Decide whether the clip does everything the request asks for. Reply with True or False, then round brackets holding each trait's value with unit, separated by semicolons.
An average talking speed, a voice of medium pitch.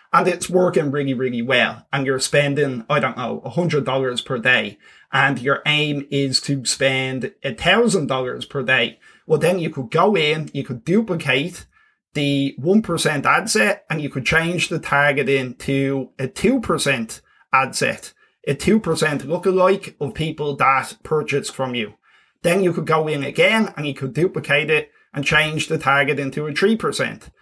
True (165 wpm; 145 Hz)